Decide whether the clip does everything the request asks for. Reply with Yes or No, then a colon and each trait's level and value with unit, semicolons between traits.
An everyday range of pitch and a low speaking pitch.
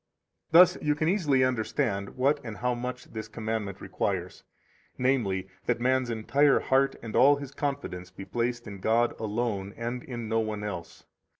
Yes: average, 3.8 semitones; low, 120 Hz